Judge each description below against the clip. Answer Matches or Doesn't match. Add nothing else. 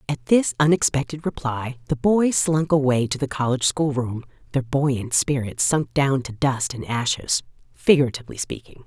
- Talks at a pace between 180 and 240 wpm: Doesn't match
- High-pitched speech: Doesn't match